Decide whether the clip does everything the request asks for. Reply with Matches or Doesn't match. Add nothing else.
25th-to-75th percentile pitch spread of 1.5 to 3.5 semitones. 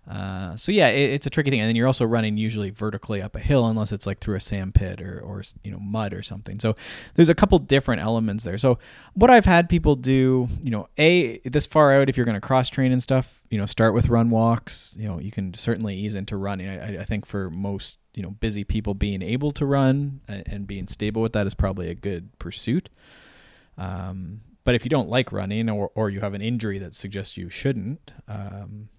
Doesn't match